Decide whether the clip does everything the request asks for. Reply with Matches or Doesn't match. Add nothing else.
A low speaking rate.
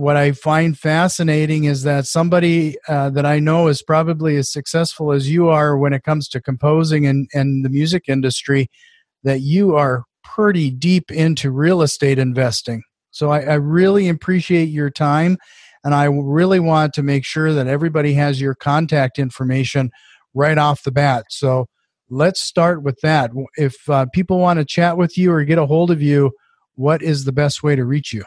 Doesn't match